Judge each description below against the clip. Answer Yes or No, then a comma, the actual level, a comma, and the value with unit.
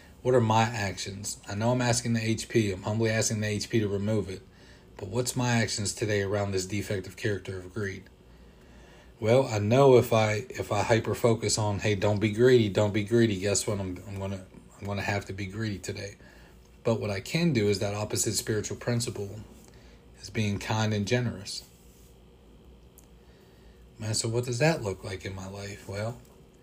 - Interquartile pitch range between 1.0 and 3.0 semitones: Yes, average, 2.7 semitones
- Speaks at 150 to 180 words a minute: No, average, 190 wpm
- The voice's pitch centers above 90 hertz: Yes, low, 105 Hz